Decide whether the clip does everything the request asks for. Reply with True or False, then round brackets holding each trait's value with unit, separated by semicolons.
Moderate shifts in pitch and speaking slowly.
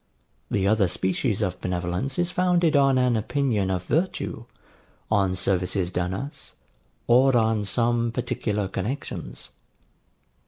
False (6.0 semitones; 120 wpm)